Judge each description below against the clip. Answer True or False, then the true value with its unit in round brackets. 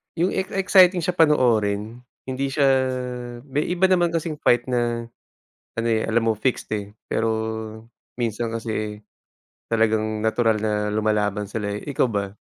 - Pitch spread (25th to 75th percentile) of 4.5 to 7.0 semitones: True (4.9 semitones)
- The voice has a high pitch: False (115 Hz)